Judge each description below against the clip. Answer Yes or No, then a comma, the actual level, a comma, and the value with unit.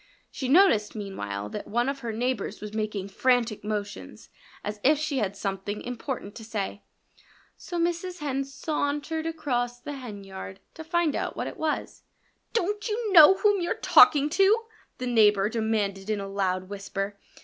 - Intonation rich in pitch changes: Yes, wide, 7.1 semitones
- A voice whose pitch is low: No, high, 240 Hz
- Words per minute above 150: Yes, average, 160 wpm